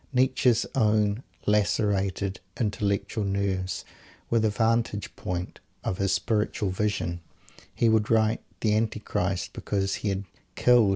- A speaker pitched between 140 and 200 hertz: No, low, 105 Hz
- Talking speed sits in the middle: No, slow, 120 wpm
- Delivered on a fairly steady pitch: Yes, narrow, 2.2 semitones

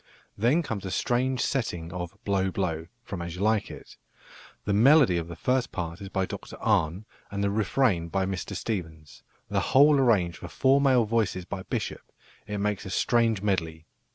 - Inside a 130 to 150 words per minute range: No, average, 180 wpm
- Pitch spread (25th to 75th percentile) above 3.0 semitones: Yes, average, 4.9 semitones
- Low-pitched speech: Yes, low, 100 Hz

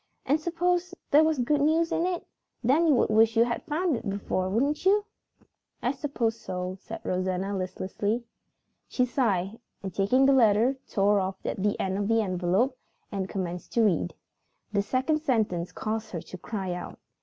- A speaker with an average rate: Yes, average, 180 wpm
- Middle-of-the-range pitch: No, high, 225 Hz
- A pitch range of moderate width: No, wide, 6.5 semitones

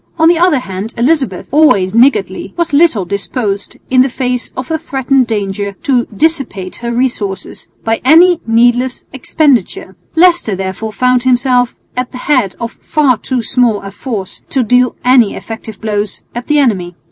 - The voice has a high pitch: Yes, high, 245 Hz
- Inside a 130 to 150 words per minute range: No, average, 160 wpm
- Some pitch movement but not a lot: Yes, average, 4.6 semitones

